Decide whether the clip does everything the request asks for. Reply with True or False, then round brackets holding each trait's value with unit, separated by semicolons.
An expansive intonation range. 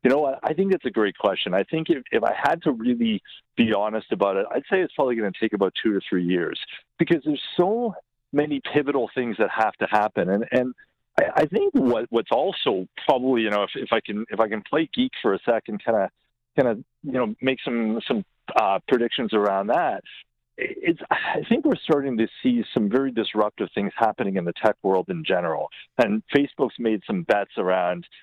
True (8.2 semitones)